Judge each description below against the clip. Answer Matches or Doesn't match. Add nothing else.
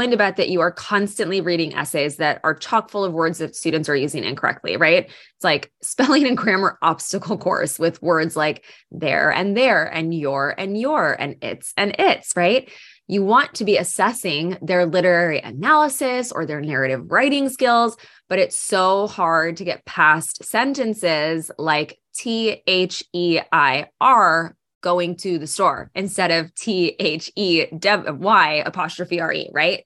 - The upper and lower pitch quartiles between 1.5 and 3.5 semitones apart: Doesn't match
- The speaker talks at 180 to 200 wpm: Doesn't match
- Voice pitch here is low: Doesn't match